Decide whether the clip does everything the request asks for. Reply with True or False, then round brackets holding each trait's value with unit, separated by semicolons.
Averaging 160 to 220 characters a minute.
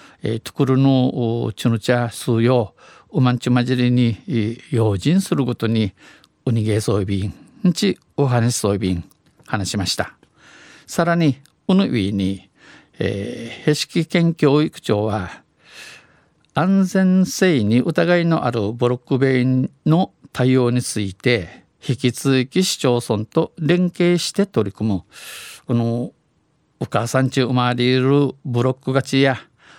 True (215 characters per minute)